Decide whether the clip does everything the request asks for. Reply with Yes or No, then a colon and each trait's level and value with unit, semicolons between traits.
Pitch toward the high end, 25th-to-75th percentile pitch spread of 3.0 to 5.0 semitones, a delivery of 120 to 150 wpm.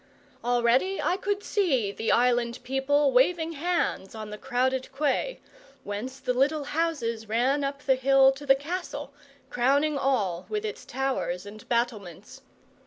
Yes: very high, 265 Hz; average, 3.7 semitones; average, 145 wpm